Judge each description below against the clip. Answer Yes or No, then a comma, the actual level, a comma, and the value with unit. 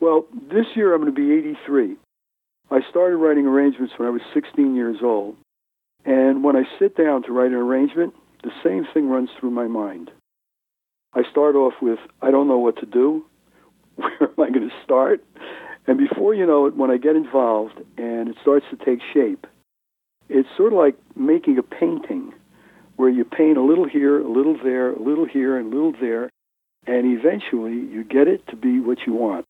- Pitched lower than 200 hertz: Yes, medium, 140 Hz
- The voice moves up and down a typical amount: No, wide, 6.3 semitones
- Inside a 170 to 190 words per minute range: No, average, 200 wpm